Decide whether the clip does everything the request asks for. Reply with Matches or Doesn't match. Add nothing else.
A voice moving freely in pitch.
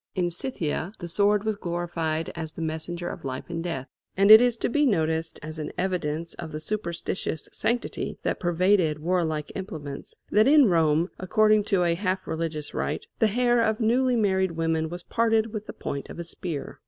Doesn't match